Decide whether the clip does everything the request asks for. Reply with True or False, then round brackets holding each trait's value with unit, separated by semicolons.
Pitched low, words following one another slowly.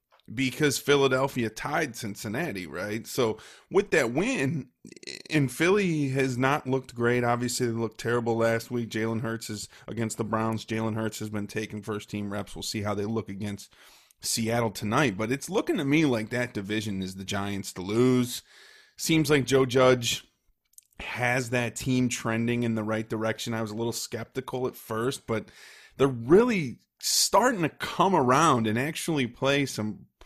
False (120 Hz; 170 wpm)